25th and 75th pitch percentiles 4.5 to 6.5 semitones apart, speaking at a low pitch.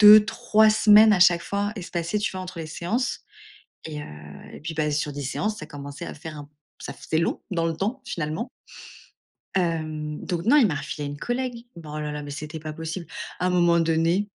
No: average, 5.1 semitones; medium, 170 Hz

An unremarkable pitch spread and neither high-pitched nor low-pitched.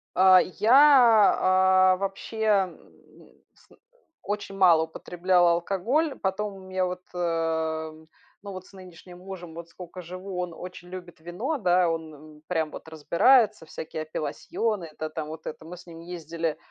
Yes: average, 3.0 semitones; medium, 180 Hz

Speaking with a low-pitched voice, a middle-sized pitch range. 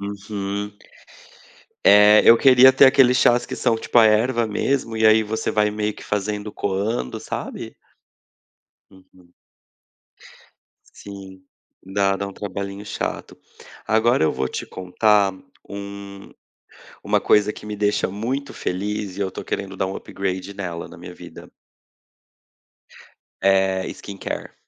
No: low, 100 Hz; narrow, 2.0 semitones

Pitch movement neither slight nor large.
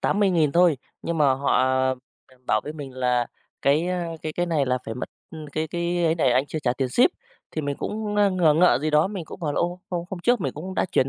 Yes: average, 4.2 semitones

